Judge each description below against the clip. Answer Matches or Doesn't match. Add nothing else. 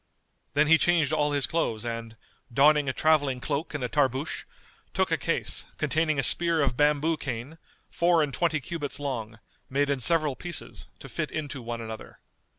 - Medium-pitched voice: Matches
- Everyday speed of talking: Matches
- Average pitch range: Matches